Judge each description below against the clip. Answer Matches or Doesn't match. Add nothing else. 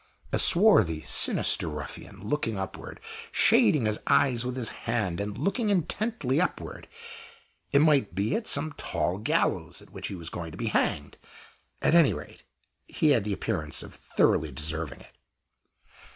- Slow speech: Doesn't match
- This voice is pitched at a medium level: Doesn't match